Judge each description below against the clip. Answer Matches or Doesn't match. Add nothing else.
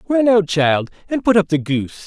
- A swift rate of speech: Matches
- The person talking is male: Matches